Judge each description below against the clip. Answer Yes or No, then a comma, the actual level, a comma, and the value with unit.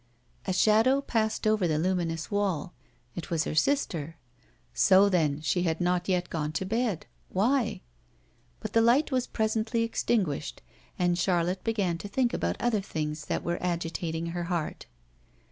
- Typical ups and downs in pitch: Yes, average, 4.8 semitones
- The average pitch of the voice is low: No, medium, 180 Hz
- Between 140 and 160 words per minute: Yes, average, 155 wpm